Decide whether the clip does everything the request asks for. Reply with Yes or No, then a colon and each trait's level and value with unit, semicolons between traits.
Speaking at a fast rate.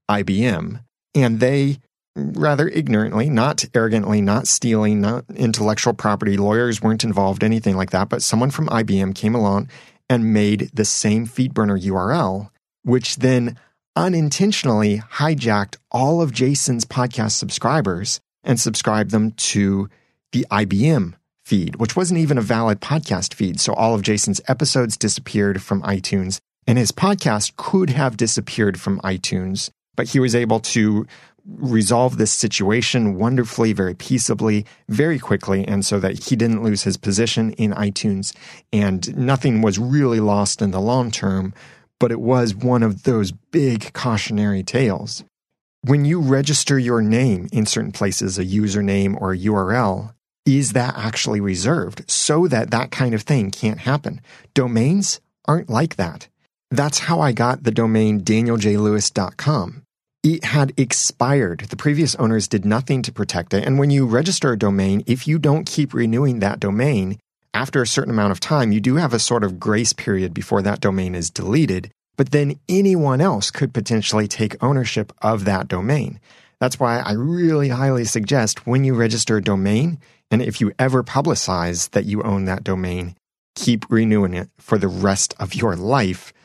No: average, 160 wpm